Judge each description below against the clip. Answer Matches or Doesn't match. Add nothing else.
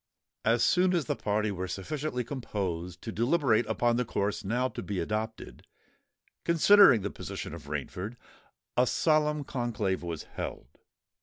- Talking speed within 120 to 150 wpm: Matches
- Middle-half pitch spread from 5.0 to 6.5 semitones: Matches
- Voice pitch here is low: Matches